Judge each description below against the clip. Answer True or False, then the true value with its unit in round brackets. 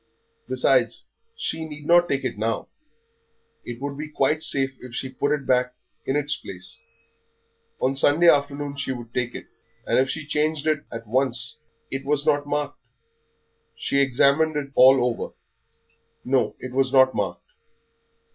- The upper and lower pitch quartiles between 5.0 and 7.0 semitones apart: False (2.7 semitones)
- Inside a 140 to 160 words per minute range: True (155 wpm)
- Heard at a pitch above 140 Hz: False (135 Hz)